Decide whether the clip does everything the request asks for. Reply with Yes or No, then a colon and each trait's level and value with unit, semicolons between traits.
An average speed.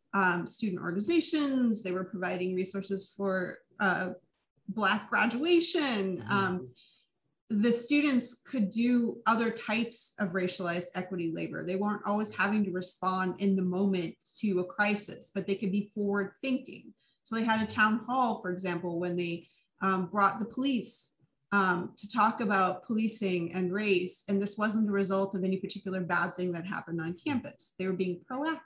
Yes: average, 165 wpm